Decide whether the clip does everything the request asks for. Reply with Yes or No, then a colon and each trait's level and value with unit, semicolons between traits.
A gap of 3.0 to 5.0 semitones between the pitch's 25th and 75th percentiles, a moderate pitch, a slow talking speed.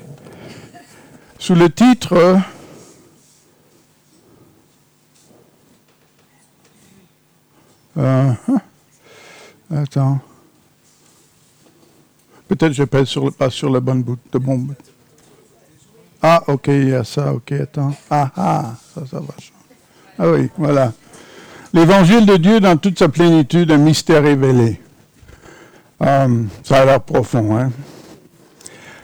Yes: average, 4.2 semitones; medium, 145 Hz; slow, 100 wpm